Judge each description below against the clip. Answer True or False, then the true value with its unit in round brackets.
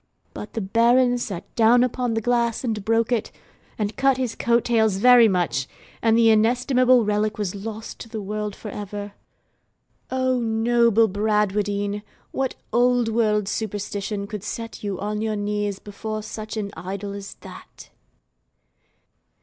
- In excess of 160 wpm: False (150 wpm)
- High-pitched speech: True (220 Hz)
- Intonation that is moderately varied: False (2.3 semitones)